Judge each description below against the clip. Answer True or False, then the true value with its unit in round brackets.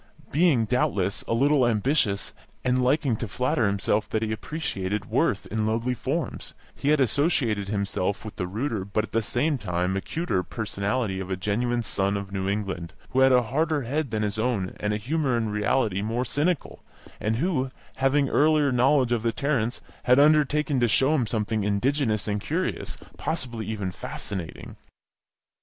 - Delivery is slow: False (170 wpm)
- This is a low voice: True (115 Hz)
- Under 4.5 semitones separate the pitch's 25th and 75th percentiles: False (4.8 semitones)